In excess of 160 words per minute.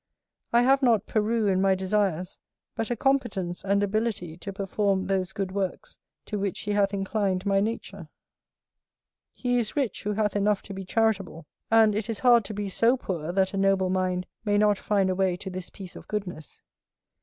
Yes: average, 190 wpm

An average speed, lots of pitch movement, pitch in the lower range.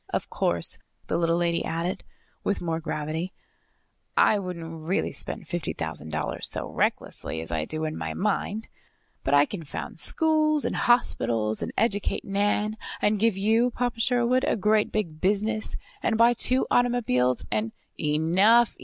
No: average, 160 wpm; wide, 6.4 semitones; high, 190 Hz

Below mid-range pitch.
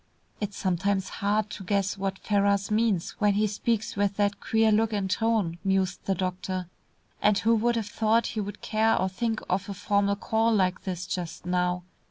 No: high, 200 Hz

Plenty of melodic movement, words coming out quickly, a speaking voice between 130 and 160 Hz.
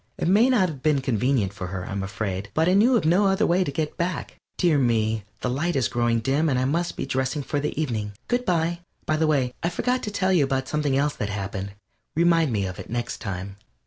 Yes: wide, 7.4 semitones; fast, 240 wpm; medium, 140 Hz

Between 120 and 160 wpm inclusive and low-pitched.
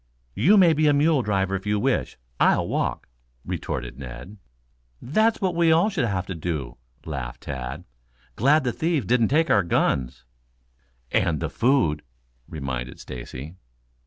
Yes: average, 150 wpm; low, 105 Hz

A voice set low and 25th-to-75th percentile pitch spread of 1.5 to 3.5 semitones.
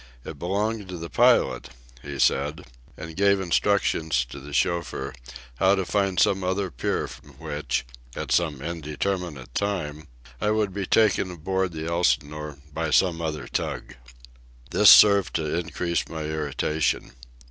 No: very low, 85 Hz; average, 4.0 semitones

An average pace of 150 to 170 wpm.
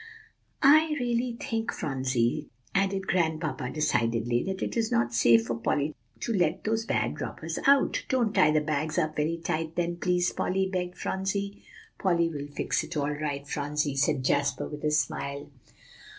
Yes: average, 165 wpm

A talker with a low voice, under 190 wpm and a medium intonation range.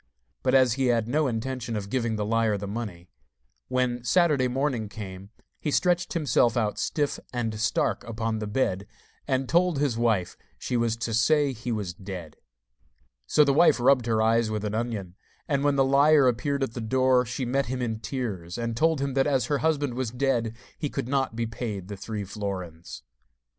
No: low, 120 Hz; average, 195 wpm; average, 3.8 semitones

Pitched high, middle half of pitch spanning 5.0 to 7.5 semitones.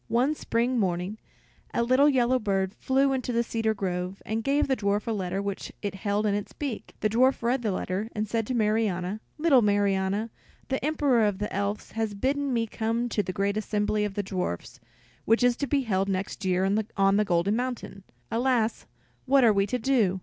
No: high, 215 Hz; average, 3.7 semitones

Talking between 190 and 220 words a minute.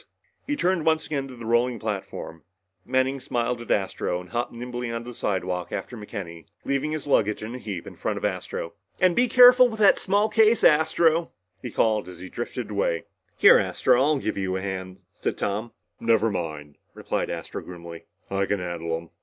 Yes: average, 195 wpm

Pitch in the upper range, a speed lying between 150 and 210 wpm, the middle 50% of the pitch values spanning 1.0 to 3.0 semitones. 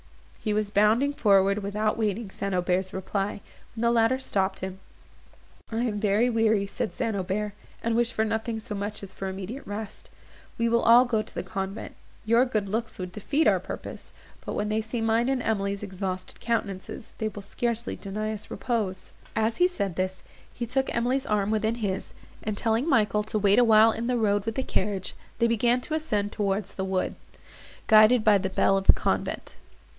Yes: high, 215 Hz; average, 190 wpm; average, 2.7 semitones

